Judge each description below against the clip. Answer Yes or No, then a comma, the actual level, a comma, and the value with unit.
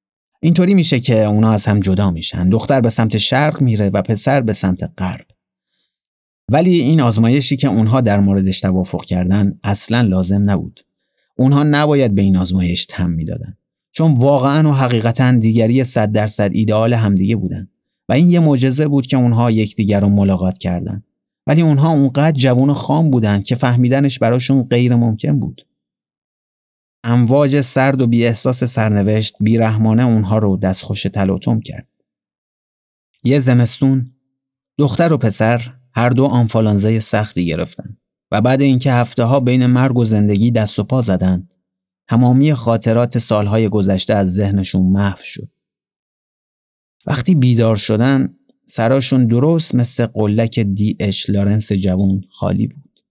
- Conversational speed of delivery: Yes, average, 145 wpm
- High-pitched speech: No, low, 115 Hz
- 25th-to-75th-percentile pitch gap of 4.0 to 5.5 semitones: Yes, average, 4.8 semitones